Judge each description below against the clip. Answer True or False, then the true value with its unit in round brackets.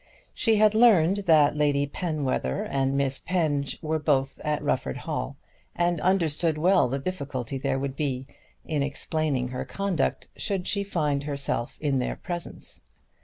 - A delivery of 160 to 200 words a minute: False (150 wpm)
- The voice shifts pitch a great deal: False (4.1 semitones)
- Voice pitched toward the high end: False (150 Hz)